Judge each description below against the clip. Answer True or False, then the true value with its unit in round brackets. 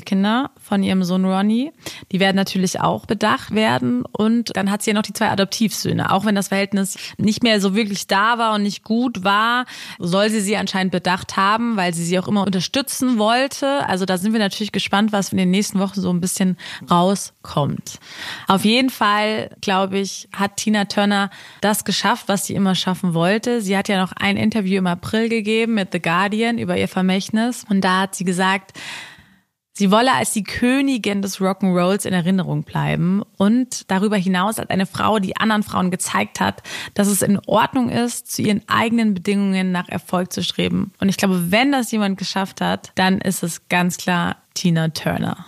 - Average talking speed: False (195 wpm)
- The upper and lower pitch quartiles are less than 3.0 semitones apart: True (2.5 semitones)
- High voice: True (200 Hz)